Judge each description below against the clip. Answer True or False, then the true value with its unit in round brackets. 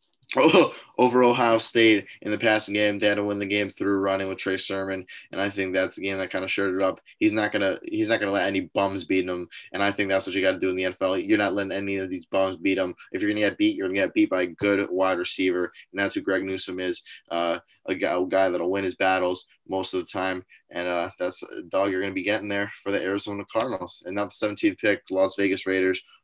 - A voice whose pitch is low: True (95 Hz)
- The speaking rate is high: True (260 wpm)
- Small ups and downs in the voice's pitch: True (1.5 semitones)